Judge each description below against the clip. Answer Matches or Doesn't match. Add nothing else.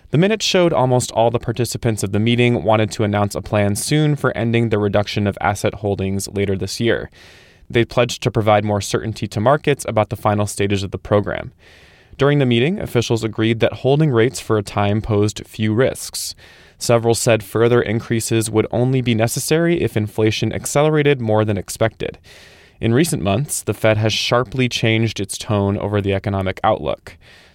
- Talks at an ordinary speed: Matches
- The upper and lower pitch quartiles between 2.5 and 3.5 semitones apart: Matches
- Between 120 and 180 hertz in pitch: Doesn't match